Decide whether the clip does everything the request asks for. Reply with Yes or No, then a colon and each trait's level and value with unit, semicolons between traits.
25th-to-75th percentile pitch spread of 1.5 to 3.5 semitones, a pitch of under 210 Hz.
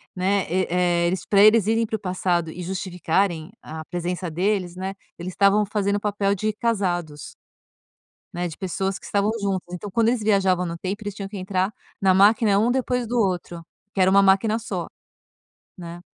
Yes: narrow, 2.6 semitones; high, 190 Hz